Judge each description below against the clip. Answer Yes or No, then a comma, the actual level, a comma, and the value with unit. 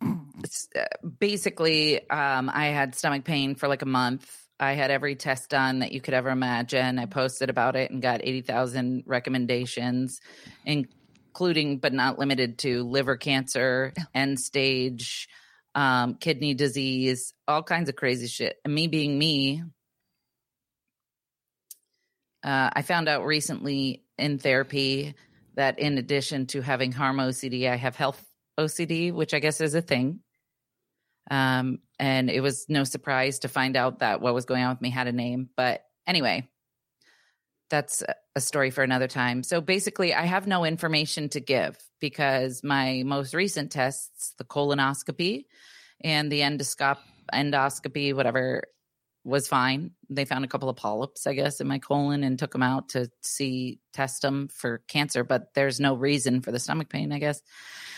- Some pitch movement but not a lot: No, narrow, 2.2 semitones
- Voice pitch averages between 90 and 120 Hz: No, low, 135 Hz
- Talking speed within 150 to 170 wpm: Yes, average, 160 wpm